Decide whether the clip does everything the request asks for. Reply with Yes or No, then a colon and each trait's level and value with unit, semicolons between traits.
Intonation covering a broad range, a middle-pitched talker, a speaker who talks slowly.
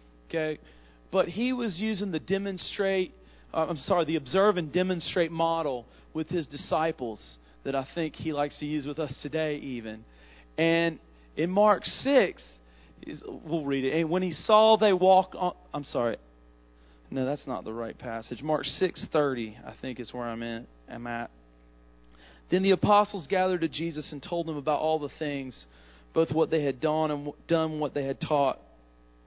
No: wide, 7.0 semitones; medium, 150 Hz; average, 175 wpm